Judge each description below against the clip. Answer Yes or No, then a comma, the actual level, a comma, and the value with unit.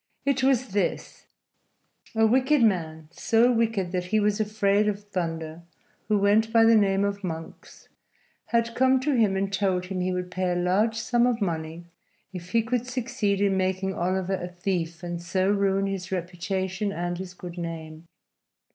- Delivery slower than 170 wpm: No, average, 175 wpm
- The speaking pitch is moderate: No, high, 195 Hz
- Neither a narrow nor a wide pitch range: Yes, average, 3.6 semitones